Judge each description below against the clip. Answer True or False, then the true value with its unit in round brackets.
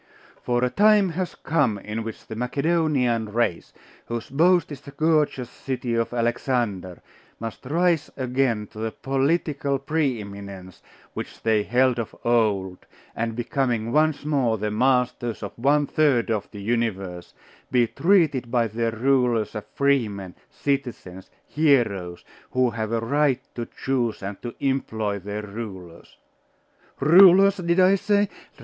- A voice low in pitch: True (120 Hz)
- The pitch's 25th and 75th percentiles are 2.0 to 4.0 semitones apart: False (4.5 semitones)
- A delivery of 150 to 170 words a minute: False (140 wpm)